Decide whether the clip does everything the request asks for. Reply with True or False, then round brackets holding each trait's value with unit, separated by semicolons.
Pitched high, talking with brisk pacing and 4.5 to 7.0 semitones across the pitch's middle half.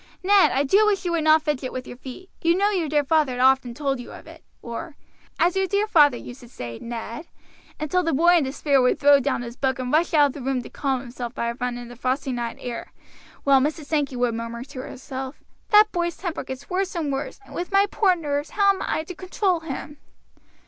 True (285 Hz; 240 wpm; 5.2 semitones)